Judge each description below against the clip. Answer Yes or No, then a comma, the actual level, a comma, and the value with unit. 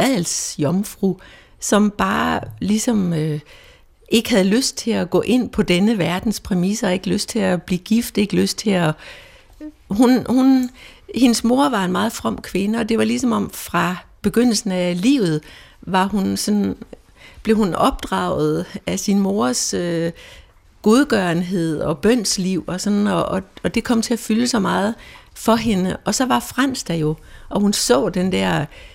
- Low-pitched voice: No, high, 205 Hz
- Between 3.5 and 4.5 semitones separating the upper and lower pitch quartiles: Yes, average, 4.2 semitones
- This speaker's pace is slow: No, average, 170 wpm